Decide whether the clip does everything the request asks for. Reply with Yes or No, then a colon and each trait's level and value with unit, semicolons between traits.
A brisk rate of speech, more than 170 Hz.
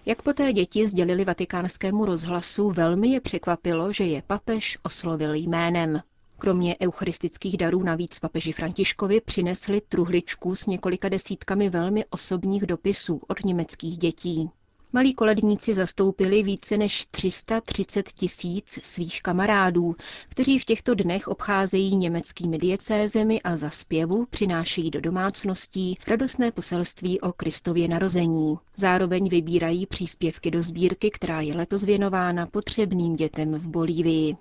No: average, 125 wpm; medium, 185 Hz